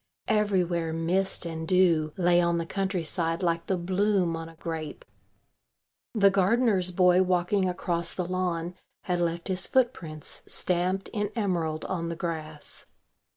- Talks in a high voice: No, medium, 175 Hz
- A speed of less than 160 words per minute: Yes, average, 140 wpm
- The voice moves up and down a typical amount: No, narrow, 2.2 semitones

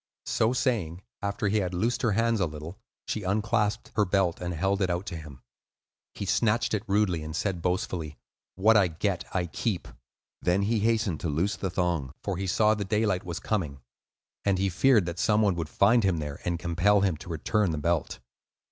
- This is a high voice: No, very low, 95 Hz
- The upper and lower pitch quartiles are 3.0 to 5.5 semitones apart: Yes, average, 3.6 semitones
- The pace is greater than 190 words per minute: Yes, average, 200 wpm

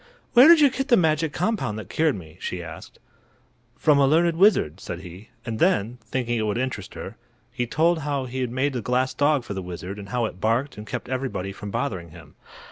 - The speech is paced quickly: Yes, fast, 220 wpm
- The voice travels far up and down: Yes, wide, 6.9 semitones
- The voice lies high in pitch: No, low, 125 Hz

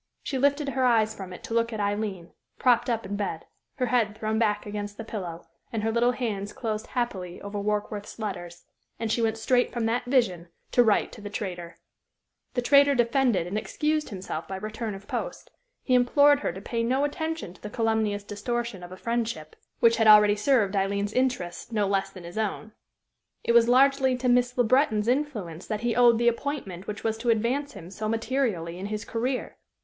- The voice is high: Yes, high, 220 Hz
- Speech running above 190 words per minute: Yes, average, 200 wpm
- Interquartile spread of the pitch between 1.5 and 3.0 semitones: No, average, 3.4 semitones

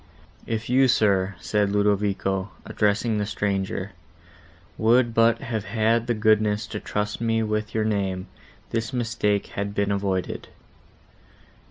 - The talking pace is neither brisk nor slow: No, slow, 130 wpm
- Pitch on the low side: Yes, low, 105 Hz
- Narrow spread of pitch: Yes, narrow, 2.0 semitones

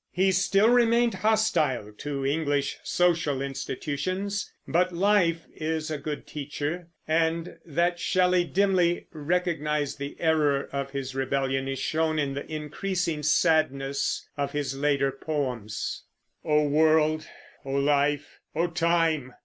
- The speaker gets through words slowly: Yes, slow, 125 wpm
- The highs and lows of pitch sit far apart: No, average, 3.7 semitones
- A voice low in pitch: No, medium, 155 Hz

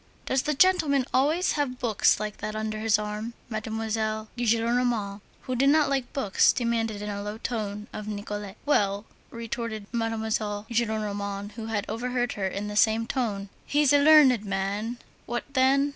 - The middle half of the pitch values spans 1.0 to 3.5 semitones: Yes, average, 3.1 semitones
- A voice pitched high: Yes, high, 225 Hz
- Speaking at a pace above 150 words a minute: Yes, average, 160 wpm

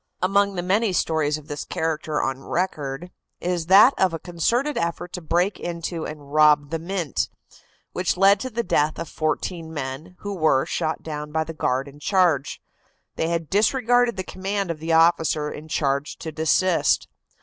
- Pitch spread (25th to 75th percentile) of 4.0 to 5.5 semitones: No, average, 3.6 semitones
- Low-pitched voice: No, medium, 165 Hz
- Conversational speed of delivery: Yes, average, 175 wpm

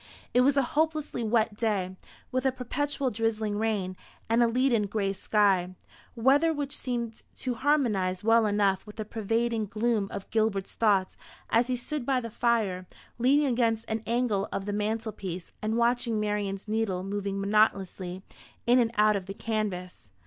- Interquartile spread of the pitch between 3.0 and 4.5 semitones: Yes, average, 3.3 semitones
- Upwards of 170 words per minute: No, average, 165 wpm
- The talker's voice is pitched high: Yes, high, 220 Hz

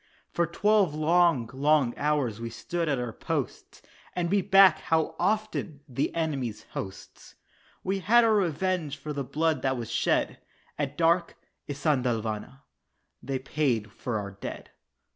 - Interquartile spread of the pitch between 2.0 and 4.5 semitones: No, wide, 5.5 semitones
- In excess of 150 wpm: No, average, 145 wpm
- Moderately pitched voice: Yes, medium, 150 Hz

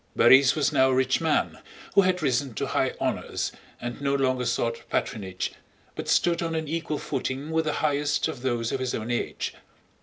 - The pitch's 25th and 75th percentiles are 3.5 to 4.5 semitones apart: Yes, average, 4.0 semitones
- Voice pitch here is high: No, low, 135 Hz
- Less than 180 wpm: No, average, 190 wpm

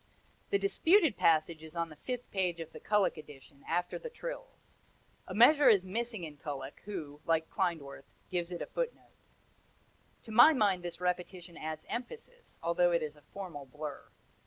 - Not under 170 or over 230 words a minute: Yes, average, 175 wpm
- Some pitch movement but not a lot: No, wide, 6.1 semitones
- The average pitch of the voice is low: No, medium, 175 Hz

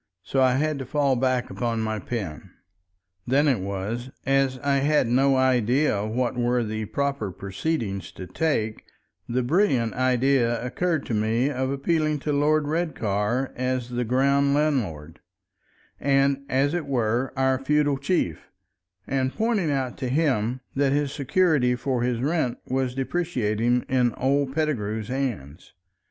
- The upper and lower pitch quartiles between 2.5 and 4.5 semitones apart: Yes, average, 3.1 semitones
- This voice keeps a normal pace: Yes, average, 145 wpm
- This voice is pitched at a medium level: No, low, 130 Hz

